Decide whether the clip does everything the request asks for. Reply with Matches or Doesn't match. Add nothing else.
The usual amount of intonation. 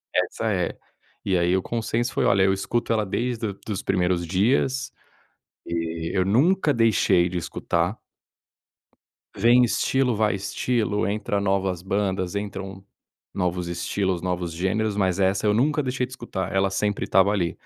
Matches